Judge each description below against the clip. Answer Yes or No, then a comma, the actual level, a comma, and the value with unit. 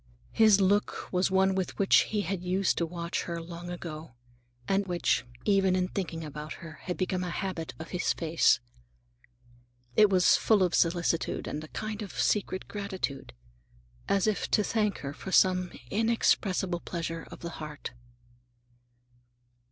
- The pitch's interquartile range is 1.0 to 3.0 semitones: Yes, average, 2.7 semitones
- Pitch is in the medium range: Yes, medium, 180 Hz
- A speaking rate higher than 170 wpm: No, average, 150 wpm